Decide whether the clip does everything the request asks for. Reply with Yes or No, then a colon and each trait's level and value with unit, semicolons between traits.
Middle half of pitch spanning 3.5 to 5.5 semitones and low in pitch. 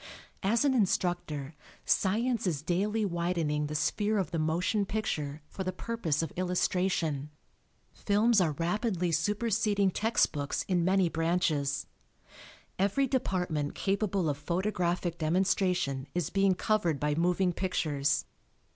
No: average, 4.1 semitones; medium, 180 Hz